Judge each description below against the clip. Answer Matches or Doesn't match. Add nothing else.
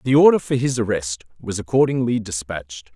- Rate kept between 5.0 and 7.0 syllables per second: Matches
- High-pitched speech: Doesn't match